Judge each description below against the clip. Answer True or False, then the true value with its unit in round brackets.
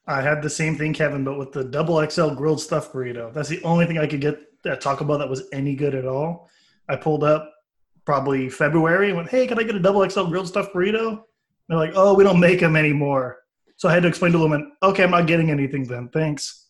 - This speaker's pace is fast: True (250 wpm)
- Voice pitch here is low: False (155 Hz)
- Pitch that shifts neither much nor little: True (3.4 semitones)